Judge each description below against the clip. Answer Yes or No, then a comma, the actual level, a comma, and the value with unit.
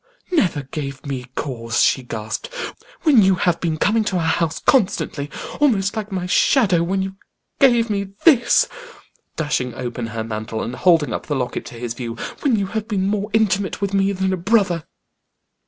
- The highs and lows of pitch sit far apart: Yes, wide, 7.5 semitones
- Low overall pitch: No, medium, 185 Hz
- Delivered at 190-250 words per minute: No, average, 180 wpm